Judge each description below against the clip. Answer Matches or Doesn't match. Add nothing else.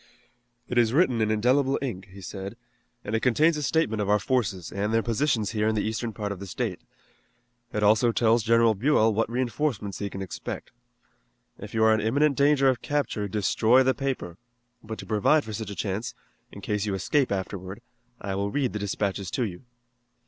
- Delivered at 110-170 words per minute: Doesn't match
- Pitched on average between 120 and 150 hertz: Doesn't match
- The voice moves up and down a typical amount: Matches